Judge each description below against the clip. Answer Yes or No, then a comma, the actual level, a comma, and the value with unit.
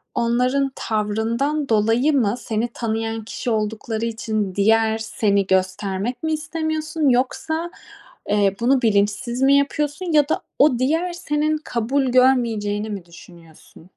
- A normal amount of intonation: Yes, average, 4.8 semitones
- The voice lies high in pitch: Yes, high, 235 Hz